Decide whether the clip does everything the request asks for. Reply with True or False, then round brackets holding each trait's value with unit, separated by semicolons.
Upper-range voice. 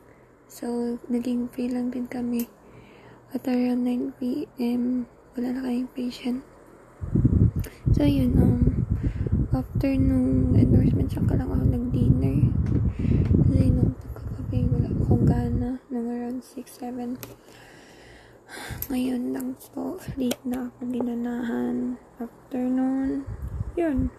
True (245 Hz)